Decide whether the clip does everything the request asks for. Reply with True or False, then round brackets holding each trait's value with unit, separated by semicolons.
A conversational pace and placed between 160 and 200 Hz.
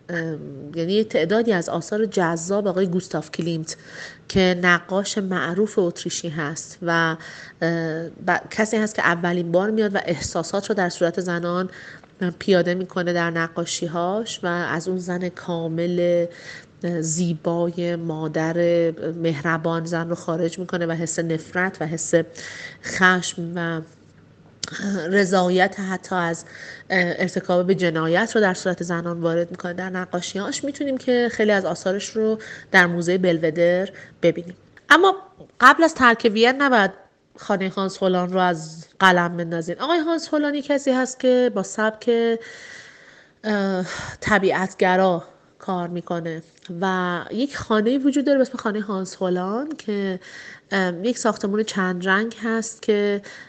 True (130 wpm; 185 Hz)